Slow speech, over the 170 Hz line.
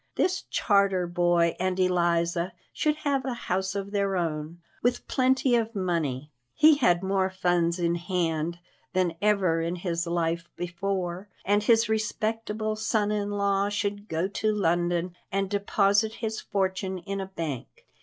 No: average, 150 wpm; high, 190 Hz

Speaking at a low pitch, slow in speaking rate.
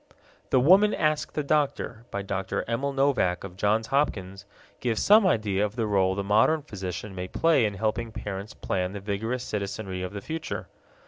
No: low, 105 Hz; average, 180 wpm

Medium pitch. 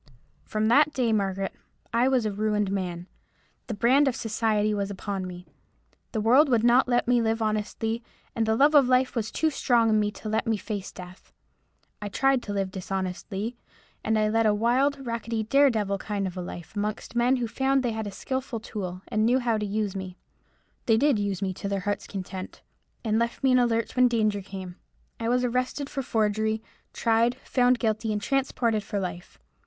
No: high, 220 Hz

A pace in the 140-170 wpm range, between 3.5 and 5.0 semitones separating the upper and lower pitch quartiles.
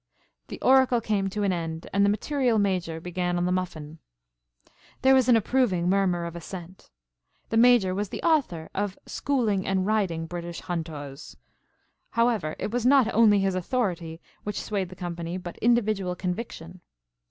Yes: average, 160 wpm; average, 4.5 semitones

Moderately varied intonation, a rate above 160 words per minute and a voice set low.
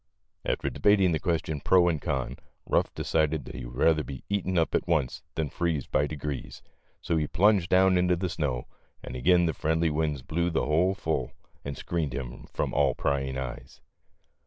Yes: average, 3.7 semitones; average, 190 wpm; very low, 80 Hz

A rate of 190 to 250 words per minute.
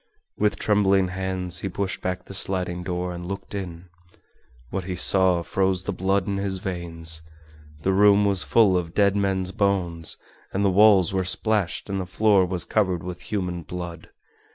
No: average, 175 wpm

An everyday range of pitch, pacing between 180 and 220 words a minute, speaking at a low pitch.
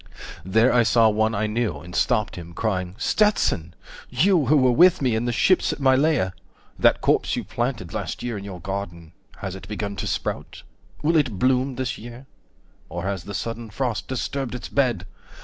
Yes: average, 5.0 semitones; average, 190 wpm; low, 115 Hz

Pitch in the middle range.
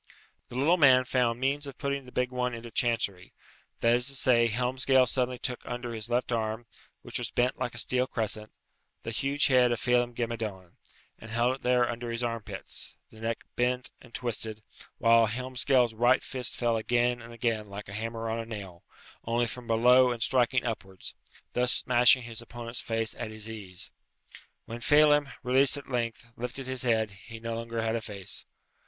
No: low, 120 Hz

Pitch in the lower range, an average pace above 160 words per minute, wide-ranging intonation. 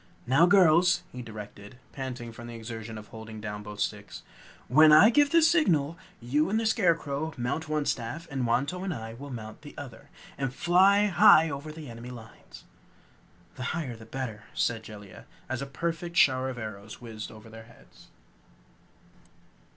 Yes: low, 130 Hz; average, 170 wpm; wide, 6.1 semitones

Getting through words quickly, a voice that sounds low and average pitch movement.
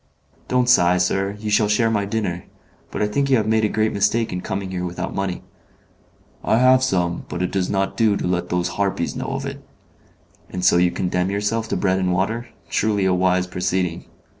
Yes: fast, 210 wpm; very low, 95 Hz; average, 3.2 semitones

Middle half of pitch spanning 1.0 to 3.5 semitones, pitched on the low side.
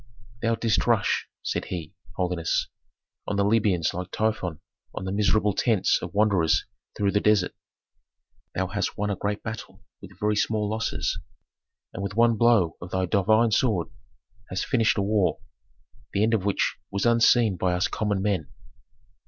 Yes: average, 2.7 semitones; low, 100 Hz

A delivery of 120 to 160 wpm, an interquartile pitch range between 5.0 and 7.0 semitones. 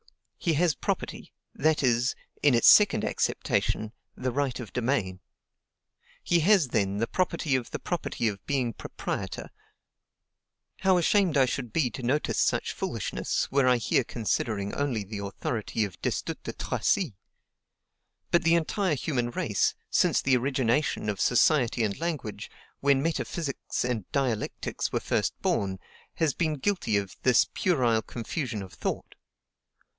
Yes: average, 145 wpm; wide, 5.6 semitones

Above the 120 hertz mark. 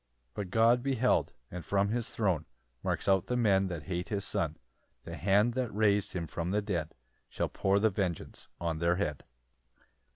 No: very low, 95 Hz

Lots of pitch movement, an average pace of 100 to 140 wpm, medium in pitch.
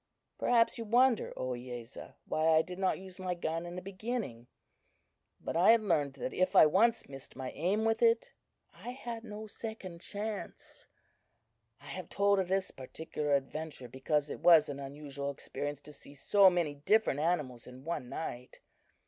No: wide, 6.3 semitones; average, 170 wpm; medium, 165 Hz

